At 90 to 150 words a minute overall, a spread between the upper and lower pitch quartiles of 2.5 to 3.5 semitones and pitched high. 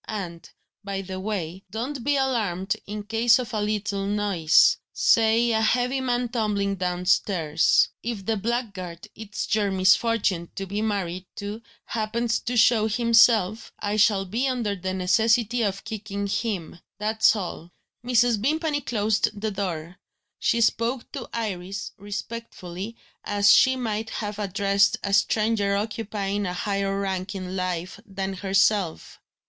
Yes: average, 140 wpm; average, 2.9 semitones; high, 205 Hz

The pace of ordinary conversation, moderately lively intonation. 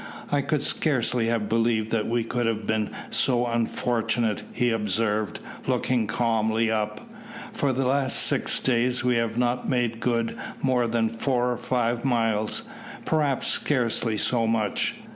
No: average, 145 wpm; narrow, 1.8 semitones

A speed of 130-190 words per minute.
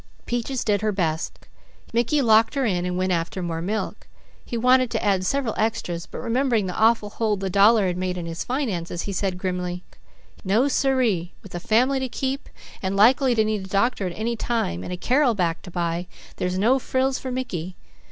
No: fast, 205 wpm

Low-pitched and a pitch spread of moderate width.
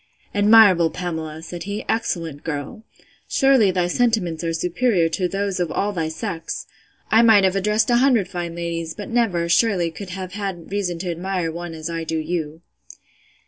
No: medium, 180 Hz; average, 3.6 semitones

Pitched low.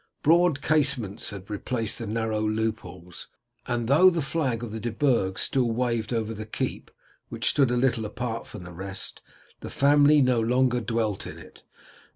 Yes: low, 115 Hz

